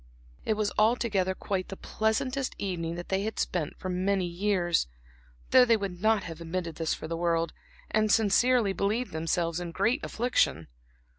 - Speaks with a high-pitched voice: Yes, high, 195 Hz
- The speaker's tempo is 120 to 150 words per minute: No, average, 165 wpm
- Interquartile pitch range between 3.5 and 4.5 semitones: Yes, average, 4.2 semitones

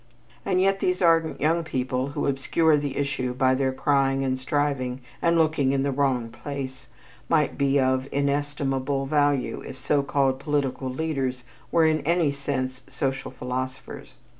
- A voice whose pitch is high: No, medium, 140 Hz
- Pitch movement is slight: Yes, narrow, 2.1 semitones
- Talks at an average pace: Yes, average, 155 wpm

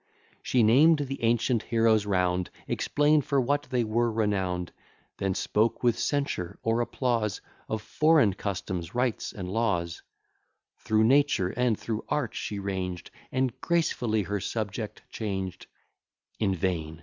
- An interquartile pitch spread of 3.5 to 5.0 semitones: Yes, average, 4.6 semitones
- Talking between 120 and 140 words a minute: Yes, slow, 135 wpm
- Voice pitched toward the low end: Yes, low, 110 Hz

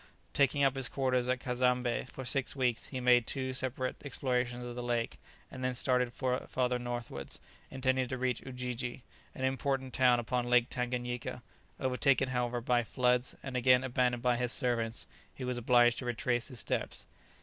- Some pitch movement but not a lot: No, narrow, 1.0 semitones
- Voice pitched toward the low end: Yes, low, 125 Hz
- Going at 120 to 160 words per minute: No, average, 170 wpm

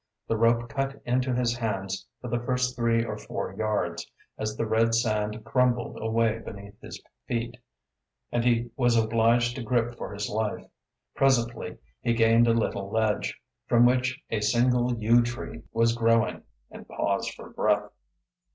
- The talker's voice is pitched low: Yes, low, 115 Hz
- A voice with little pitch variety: Yes, narrow, 1.6 semitones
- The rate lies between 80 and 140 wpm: No, average, 160 wpm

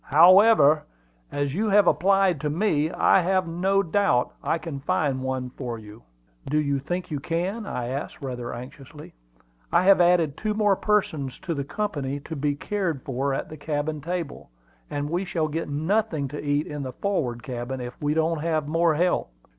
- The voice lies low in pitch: No, medium, 155 Hz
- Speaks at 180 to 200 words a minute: Yes, average, 185 wpm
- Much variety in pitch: No, average, 4.5 semitones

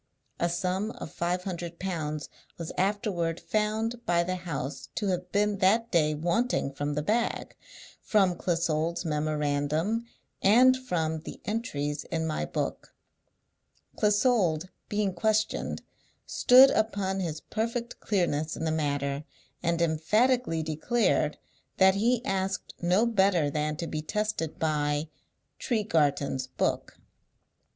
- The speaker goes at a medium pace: No, slow, 125 wpm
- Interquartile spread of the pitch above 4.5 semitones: Yes, wide, 5.4 semitones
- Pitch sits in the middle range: Yes, medium, 175 Hz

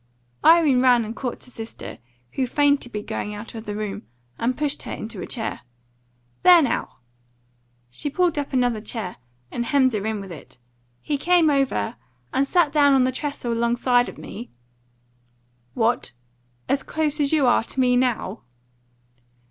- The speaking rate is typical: Yes, average, 170 wpm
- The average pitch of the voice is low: No, very high, 250 Hz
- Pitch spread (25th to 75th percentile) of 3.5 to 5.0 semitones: Yes, average, 4.4 semitones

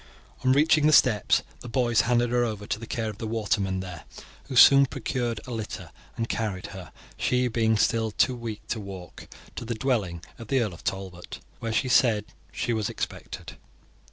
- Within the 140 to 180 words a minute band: No, average, 190 wpm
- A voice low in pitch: Yes, low, 115 Hz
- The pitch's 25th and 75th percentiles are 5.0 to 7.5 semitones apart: No, average, 3.1 semitones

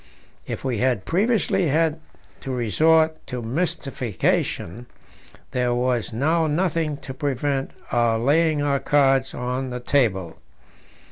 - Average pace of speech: No, slow, 120 wpm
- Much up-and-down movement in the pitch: No, average, 4.2 semitones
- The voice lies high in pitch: No, low, 135 Hz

